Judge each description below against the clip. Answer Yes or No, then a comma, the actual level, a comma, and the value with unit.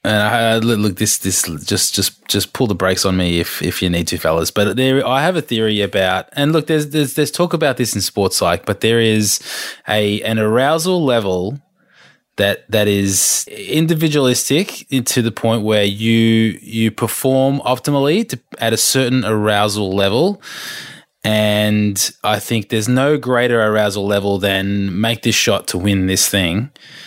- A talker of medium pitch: No, low, 110 Hz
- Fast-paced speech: No, average, 175 wpm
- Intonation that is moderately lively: Yes, average, 4.2 semitones